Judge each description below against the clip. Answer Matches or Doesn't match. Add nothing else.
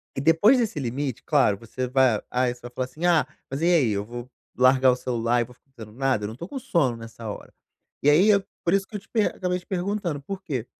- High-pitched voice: Doesn't match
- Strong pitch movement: Matches